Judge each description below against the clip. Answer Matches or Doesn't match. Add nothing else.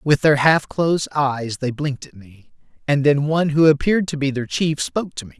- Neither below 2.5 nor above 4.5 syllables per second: Doesn't match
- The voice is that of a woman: Doesn't match